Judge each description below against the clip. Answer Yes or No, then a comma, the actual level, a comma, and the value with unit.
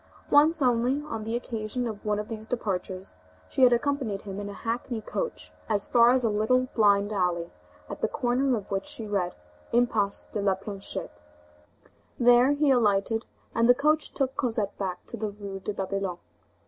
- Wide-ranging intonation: No, average, 3.7 semitones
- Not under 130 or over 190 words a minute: Yes, average, 180 wpm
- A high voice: Yes, high, 220 Hz